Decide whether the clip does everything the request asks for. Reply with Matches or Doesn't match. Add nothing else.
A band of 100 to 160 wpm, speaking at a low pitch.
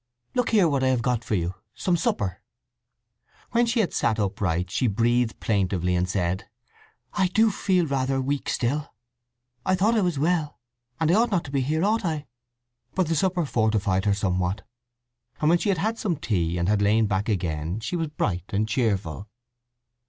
Doesn't match